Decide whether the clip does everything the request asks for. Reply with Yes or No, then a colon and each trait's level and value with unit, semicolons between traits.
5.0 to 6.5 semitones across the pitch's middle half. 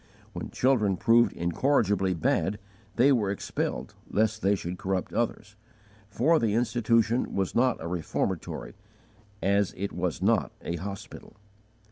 No: average, 3.7 semitones